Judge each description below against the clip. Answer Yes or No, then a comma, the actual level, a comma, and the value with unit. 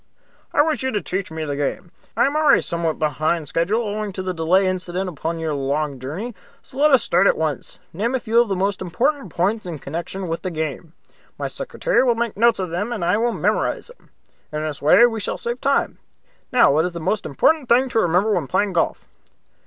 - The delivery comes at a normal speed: No, fast, 225 wpm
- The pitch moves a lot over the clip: Yes, wide, 6.4 semitones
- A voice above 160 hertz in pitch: Yes, medium, 185 Hz